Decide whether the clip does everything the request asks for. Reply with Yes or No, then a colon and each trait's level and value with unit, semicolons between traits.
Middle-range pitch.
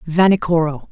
Yes: medium, 165 Hz